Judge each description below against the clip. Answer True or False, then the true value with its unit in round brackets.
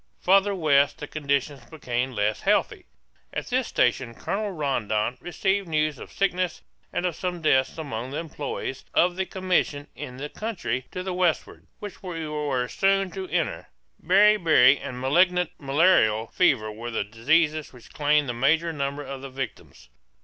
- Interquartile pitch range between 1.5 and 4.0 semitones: False (5.5 semitones)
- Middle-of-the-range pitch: True (150 Hz)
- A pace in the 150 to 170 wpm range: True (160 wpm)